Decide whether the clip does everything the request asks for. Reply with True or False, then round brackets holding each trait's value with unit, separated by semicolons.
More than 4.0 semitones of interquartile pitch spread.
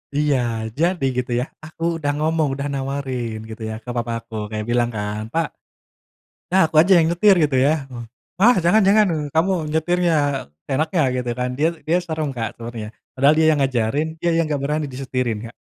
True (4.8 semitones)